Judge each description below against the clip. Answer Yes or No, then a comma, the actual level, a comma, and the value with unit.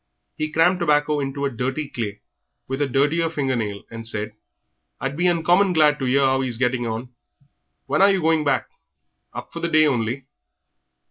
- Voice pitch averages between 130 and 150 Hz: Yes, medium, 140 Hz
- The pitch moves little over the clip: No, average, 4.0 semitones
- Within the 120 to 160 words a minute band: No, average, 190 wpm